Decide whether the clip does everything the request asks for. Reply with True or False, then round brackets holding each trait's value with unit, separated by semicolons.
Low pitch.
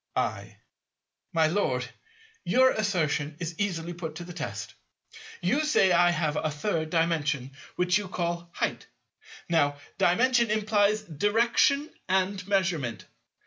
False (175 Hz)